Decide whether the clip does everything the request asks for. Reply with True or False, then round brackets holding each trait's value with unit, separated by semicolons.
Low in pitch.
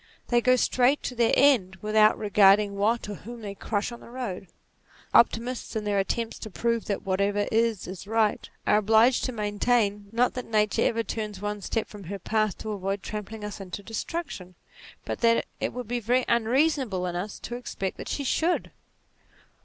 False (215 Hz)